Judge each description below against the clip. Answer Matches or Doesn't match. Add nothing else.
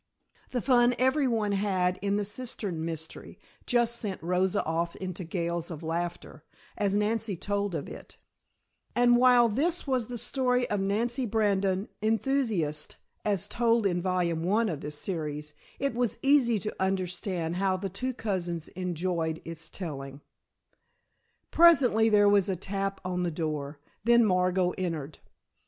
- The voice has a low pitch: Doesn't match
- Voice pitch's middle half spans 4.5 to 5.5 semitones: Matches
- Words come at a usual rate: Matches